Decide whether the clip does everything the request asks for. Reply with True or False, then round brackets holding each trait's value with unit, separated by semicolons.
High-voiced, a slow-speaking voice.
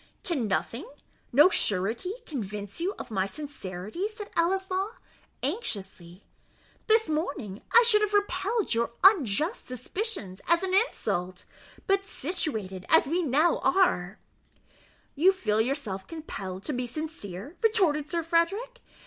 True (305 Hz; 130 wpm)